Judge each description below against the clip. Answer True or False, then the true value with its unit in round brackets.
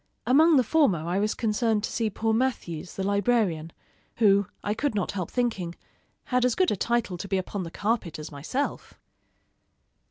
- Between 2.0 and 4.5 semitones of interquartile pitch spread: False (4.9 semitones)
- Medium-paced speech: True (180 wpm)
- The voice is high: True (210 Hz)